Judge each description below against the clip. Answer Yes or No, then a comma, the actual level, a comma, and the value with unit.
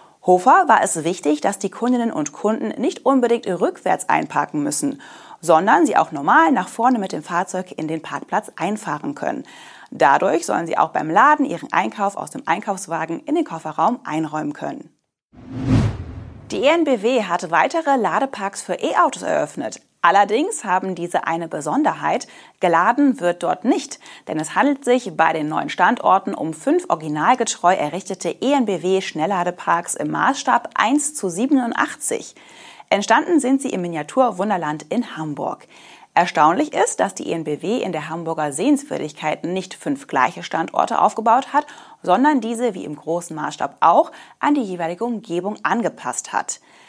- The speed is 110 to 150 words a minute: Yes, average, 145 wpm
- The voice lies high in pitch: Yes, high, 200 Hz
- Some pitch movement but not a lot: No, wide, 8.2 semitones